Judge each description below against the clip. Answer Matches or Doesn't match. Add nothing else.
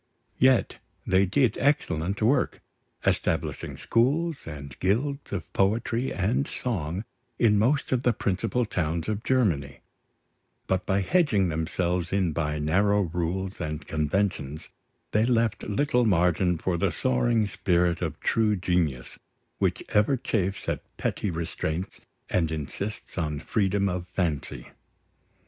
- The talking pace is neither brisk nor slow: Doesn't match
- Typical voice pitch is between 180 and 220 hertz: Doesn't match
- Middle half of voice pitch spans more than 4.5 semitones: Matches